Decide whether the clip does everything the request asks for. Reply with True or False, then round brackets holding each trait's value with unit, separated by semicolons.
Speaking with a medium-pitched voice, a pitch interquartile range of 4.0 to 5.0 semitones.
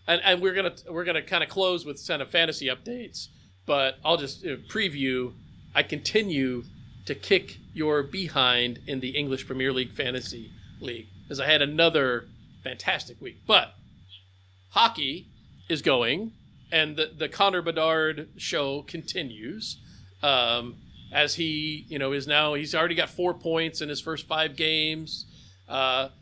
True (145 Hz; 4.3 semitones)